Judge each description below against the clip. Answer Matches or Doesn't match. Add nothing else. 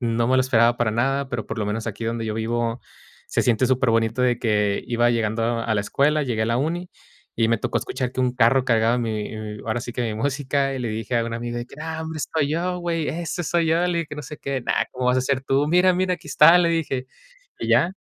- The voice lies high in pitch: Doesn't match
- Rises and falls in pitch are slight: Doesn't match